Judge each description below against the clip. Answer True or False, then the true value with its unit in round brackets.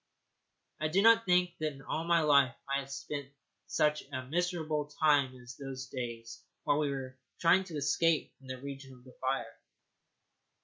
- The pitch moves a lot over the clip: False (3.2 semitones)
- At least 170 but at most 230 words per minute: True (180 wpm)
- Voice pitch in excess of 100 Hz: True (140 Hz)